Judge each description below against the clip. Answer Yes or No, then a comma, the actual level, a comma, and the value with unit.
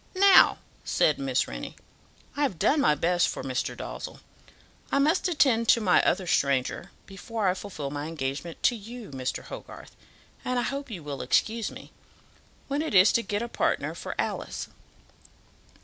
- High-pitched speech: Yes, high, 200 Hz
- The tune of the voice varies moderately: No, wide, 8.9 semitones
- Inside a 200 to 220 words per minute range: No, average, 165 wpm